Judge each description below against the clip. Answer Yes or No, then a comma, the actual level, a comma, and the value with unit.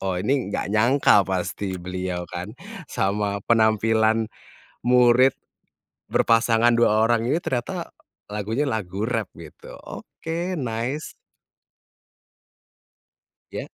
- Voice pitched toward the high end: No, low, 110 Hz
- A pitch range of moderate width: Yes, average, 3.4 semitones